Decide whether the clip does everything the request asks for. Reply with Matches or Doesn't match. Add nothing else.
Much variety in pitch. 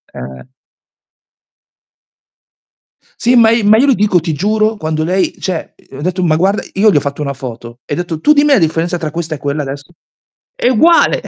Matches